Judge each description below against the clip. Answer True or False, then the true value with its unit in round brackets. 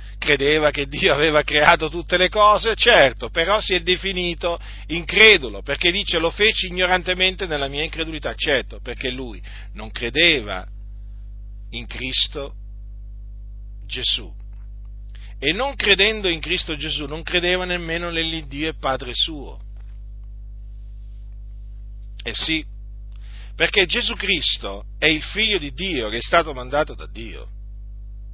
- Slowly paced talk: False (125 wpm)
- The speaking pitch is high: False (140 Hz)